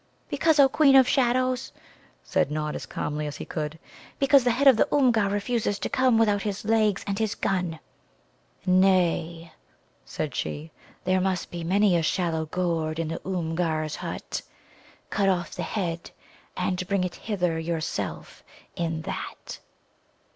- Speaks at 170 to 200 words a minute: No, average, 155 wpm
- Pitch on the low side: No, medium, 185 Hz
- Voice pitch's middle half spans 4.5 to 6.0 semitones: Yes, average, 5.1 semitones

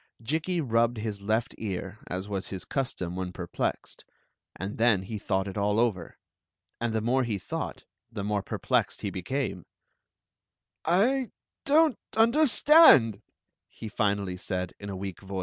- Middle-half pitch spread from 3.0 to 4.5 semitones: No, average, 5.0 semitones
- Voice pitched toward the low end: Yes, low, 105 Hz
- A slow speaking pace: No, average, 145 wpm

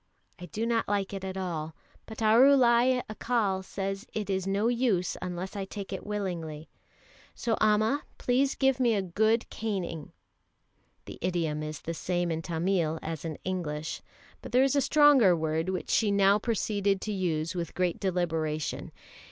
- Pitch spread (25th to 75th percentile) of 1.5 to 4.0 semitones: No, average, 4.5 semitones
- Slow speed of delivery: No, average, 165 wpm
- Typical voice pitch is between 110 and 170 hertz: No, high, 195 Hz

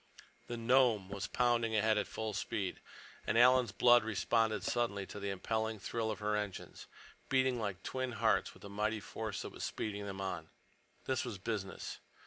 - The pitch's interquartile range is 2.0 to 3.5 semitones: Yes, average, 2.8 semitones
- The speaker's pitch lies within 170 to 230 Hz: No, low, 110 Hz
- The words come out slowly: No, average, 175 wpm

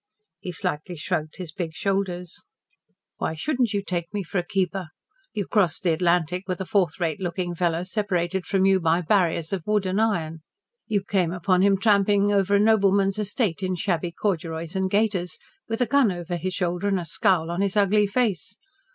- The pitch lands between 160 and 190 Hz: Yes, medium, 185 Hz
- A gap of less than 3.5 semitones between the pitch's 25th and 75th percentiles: Yes, average, 2.7 semitones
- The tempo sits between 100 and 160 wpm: No, average, 190 wpm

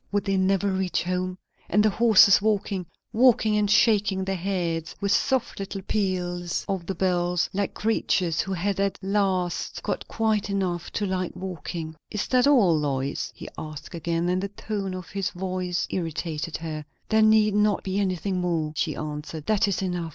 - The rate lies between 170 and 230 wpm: Yes, average, 175 wpm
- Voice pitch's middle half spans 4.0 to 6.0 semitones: No, narrow, 2.6 semitones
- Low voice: No, high, 190 Hz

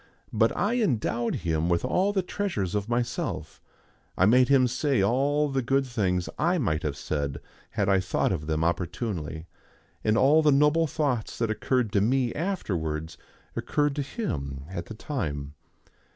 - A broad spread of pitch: Yes, wide, 8.7 semitones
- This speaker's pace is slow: No, average, 165 wpm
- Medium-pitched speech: No, low, 115 Hz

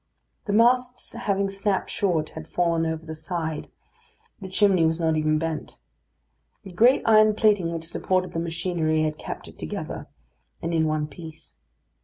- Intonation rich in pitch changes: No, average, 3.8 semitones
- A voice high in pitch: No, medium, 170 Hz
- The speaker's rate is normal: Yes, average, 160 wpm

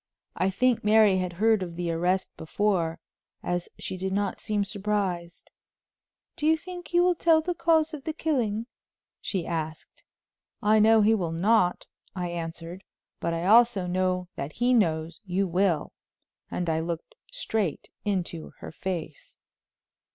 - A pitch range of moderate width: Yes, average, 4.5 semitones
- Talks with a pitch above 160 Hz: Yes, high, 190 Hz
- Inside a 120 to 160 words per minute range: Yes, average, 150 wpm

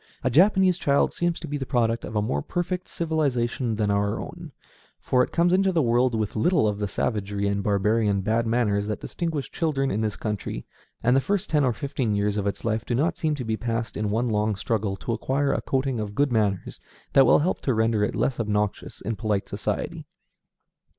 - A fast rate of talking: Yes, fast, 215 wpm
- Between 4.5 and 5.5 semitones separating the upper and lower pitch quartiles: Yes, average, 5.1 semitones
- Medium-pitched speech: No, low, 115 Hz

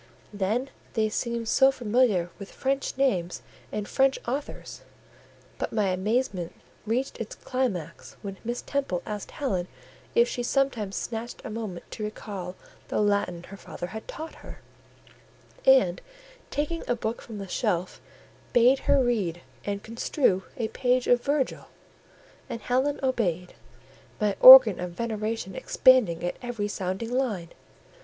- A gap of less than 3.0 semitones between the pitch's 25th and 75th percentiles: No, average, 4.9 semitones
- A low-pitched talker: No, high, 225 Hz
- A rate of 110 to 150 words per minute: Yes, average, 140 wpm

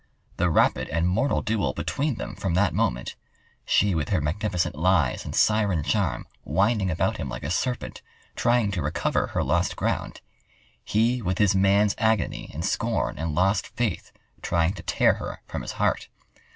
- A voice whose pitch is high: No, very low, 95 Hz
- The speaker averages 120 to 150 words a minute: No, average, 165 wpm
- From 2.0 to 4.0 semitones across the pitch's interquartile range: No, average, 4.4 semitones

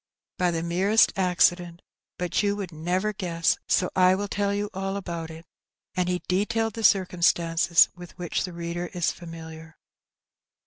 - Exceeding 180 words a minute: No, average, 165 wpm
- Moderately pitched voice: Yes, medium, 180 Hz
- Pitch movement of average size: No, narrow, 2.3 semitones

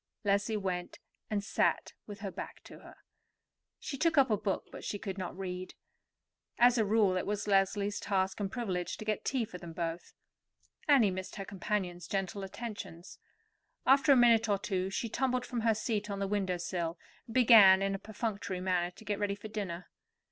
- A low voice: No, high, 200 Hz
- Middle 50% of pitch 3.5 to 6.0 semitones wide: No, average, 2.7 semitones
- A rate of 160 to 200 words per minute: Yes, average, 195 wpm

